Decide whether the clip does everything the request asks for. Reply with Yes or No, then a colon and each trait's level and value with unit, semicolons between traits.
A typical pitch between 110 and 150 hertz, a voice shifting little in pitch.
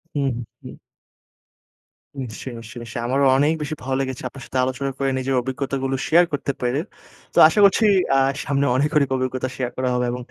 Yes: low, 135 Hz; narrow, 1.7 semitones